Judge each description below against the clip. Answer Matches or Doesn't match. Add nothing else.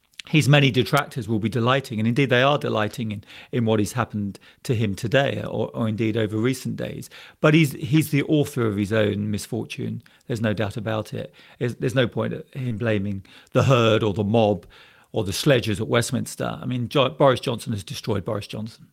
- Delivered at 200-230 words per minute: Matches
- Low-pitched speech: Matches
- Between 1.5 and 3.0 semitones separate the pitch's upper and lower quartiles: Doesn't match